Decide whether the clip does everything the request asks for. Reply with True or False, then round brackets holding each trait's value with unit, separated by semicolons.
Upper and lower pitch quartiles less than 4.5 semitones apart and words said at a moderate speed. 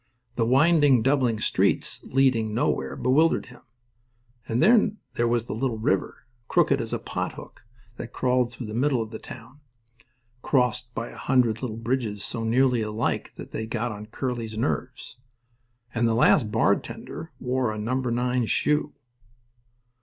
True (2.5 semitones; 155 wpm)